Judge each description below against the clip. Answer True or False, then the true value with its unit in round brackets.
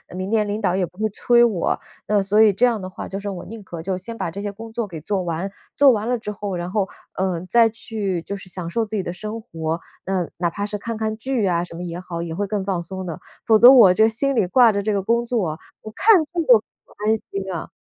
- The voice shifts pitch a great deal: False (3.5 semitones)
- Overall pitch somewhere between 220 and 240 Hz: False (200 Hz)